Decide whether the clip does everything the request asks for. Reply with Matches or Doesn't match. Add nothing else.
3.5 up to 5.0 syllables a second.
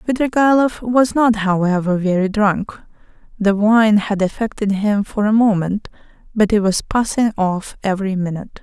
Matches